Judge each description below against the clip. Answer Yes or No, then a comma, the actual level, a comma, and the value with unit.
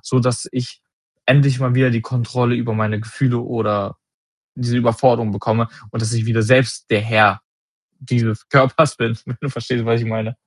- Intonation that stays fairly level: Yes, narrow, 2.2 semitones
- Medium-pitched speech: No, low, 120 Hz